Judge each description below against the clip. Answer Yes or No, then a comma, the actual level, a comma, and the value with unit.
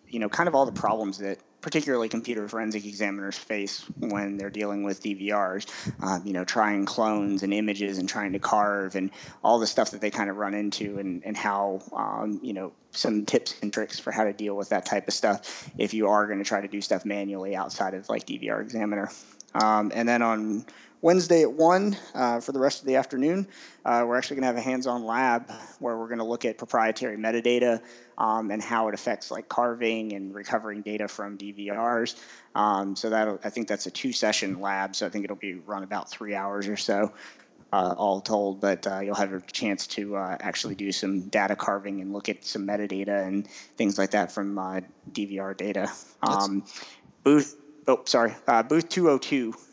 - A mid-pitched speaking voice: No, low, 105 Hz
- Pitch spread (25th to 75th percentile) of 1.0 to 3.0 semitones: Yes, narrow, 2.6 semitones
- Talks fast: Yes, fast, 210 wpm